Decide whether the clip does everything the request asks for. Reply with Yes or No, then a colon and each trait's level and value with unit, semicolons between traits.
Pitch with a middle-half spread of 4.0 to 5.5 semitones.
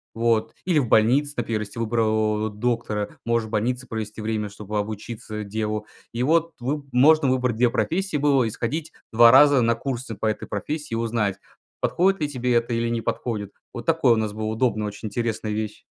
No: average, 3.0 semitones